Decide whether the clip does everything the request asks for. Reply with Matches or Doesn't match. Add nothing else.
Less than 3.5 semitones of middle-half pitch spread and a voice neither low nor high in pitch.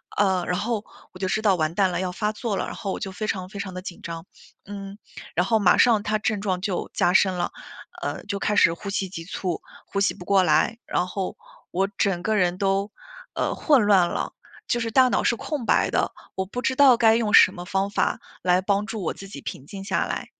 Doesn't match